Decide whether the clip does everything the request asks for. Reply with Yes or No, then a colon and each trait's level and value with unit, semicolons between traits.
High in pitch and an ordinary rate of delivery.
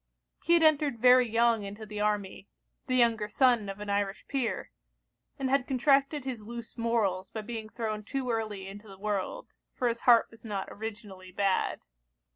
Yes: high, 225 Hz; average, 175 wpm